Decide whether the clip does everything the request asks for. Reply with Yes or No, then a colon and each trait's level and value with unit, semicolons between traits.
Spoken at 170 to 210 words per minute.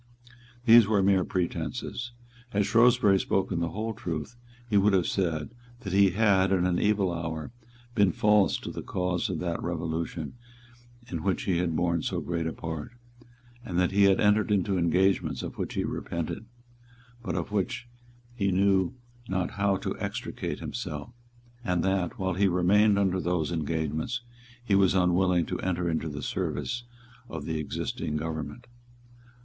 No: average, 160 wpm